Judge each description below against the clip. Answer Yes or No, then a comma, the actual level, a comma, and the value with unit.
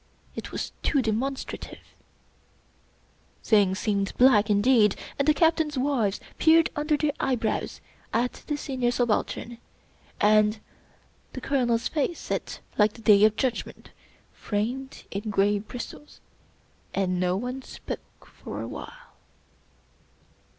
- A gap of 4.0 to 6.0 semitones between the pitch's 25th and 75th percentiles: Yes, average, 4.6 semitones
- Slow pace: Yes, slow, 120 wpm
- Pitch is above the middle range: Yes, high, 240 Hz